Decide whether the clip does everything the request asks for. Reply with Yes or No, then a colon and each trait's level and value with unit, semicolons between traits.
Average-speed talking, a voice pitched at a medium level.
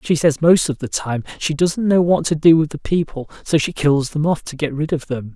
No: fast, 280 wpm; medium, 150 Hz